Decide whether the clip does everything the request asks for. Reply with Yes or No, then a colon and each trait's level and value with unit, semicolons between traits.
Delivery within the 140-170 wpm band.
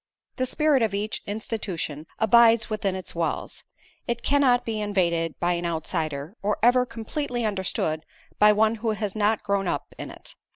Yes: average, 165 wpm